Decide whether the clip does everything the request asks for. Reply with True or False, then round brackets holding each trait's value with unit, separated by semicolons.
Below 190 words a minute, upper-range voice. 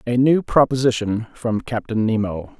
False (140 wpm; 115 Hz)